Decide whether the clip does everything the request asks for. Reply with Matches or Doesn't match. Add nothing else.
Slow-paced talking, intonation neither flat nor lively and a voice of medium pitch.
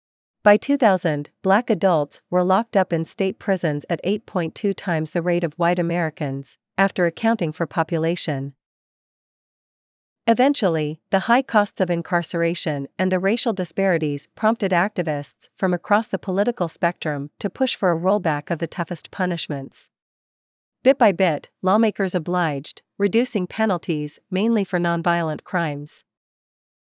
Matches